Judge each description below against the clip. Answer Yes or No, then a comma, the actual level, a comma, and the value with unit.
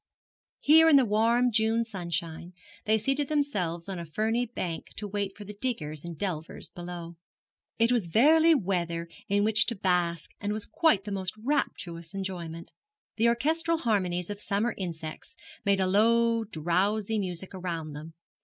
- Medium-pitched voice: No, high, 200 Hz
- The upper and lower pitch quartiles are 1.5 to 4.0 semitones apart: No, average, 5.1 semitones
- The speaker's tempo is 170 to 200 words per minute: No, average, 155 wpm